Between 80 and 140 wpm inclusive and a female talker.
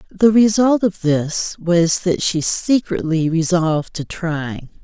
Yes: slow, 135 wpm; female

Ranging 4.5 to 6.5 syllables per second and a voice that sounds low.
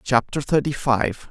No: 4.1 syllables/s; low, 130 Hz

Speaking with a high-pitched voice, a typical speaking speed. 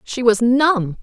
Yes: high, 240 Hz; average, 175 wpm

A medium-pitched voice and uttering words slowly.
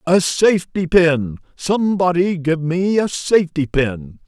Yes: medium, 170 Hz; slow, 125 wpm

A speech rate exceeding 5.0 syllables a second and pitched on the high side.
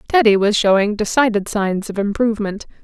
Yes: 5.5 syllables/s; high, 210 Hz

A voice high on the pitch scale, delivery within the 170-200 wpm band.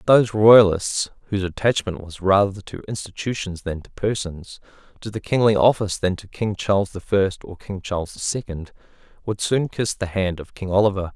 No: low, 100 Hz; average, 185 wpm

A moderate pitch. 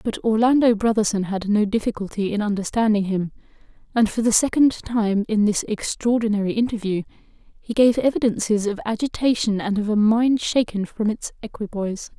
No: high, 215 Hz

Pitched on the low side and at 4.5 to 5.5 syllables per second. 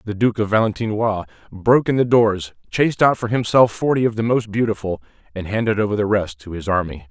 No: low, 105 Hz; 6.0 syllables/s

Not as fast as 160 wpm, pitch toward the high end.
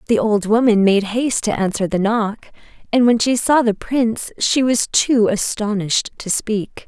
No: average, 185 wpm; high, 220 Hz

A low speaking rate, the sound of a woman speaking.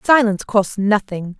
Yes: slow, 130 wpm; female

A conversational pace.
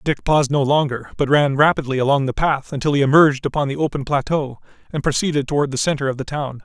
No: fast, 225 wpm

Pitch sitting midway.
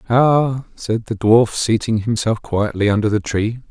No: low, 110 Hz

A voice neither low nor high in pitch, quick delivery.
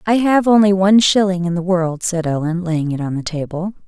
Yes: medium, 180 Hz; fast, 230 wpm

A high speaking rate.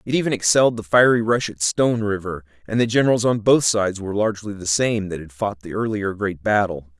Yes: fast, 225 wpm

